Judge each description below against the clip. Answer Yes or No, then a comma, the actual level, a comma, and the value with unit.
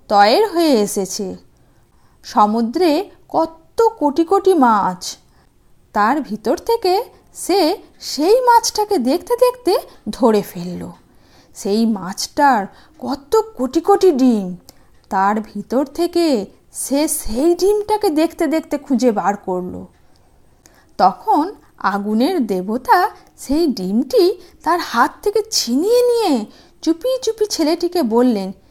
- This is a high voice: Yes, very high, 305 Hz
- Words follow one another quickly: No, average, 100 wpm